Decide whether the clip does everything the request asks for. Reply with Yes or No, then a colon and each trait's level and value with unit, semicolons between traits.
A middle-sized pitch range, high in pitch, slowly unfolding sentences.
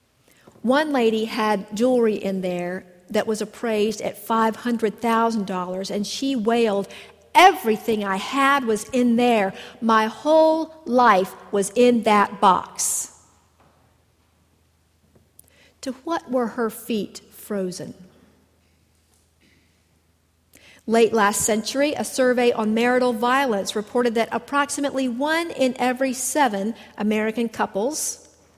Yes: average, 4.4 semitones; high, 220 Hz; slow, 105 wpm